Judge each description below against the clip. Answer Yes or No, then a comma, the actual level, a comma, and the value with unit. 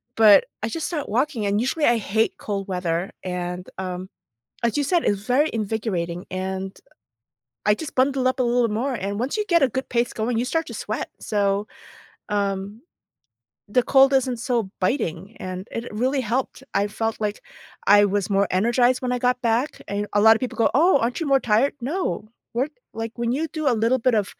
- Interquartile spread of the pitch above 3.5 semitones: Yes, average, 4.2 semitones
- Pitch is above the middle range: Yes, high, 230 Hz